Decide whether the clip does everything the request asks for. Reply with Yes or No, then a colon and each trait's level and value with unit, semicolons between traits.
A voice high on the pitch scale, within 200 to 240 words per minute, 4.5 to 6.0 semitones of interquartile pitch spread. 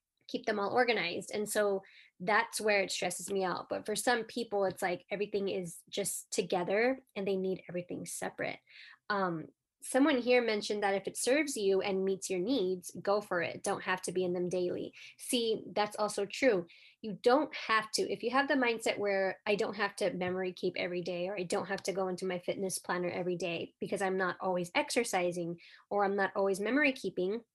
No: high, 195 Hz; fast, 205 wpm; average, 2.9 semitones